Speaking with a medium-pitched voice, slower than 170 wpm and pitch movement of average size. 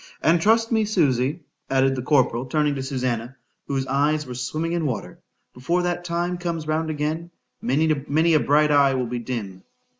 Yes: medium, 150 Hz; average, 160 wpm; average, 4.3 semitones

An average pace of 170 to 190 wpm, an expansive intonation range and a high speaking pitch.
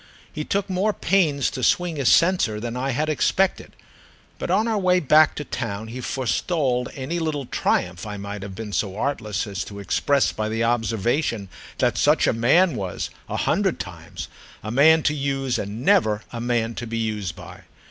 No: average, 180 wpm; wide, 6.1 semitones; low, 125 Hz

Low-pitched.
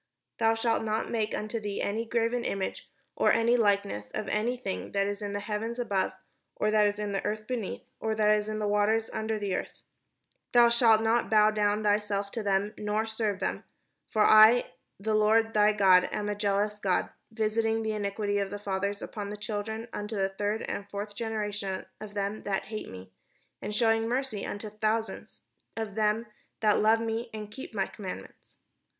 No: high, 210 Hz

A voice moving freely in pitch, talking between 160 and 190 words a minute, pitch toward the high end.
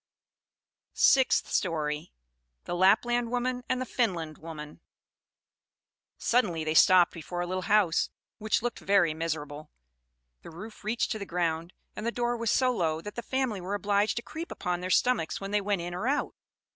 Yes: wide, 6.0 semitones; average, 170 wpm; high, 195 Hz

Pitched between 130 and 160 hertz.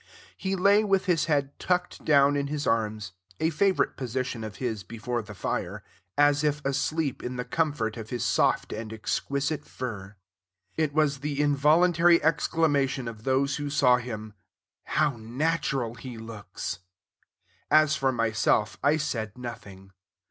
Yes: low, 135 Hz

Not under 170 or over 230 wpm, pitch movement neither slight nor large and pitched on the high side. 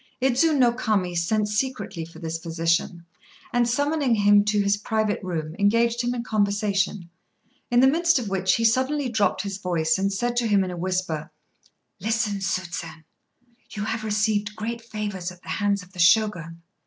Yes: average, 175 wpm; average, 4.2 semitones; high, 205 Hz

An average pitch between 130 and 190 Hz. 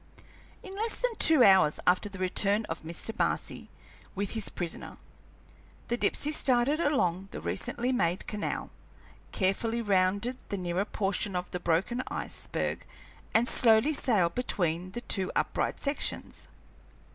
No: high, 205 Hz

